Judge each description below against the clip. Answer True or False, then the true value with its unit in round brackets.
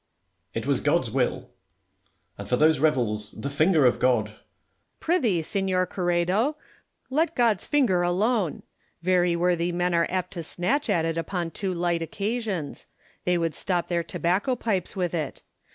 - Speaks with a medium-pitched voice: True (175 Hz)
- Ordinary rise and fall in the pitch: True (3.1 semitones)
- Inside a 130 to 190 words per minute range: True (170 wpm)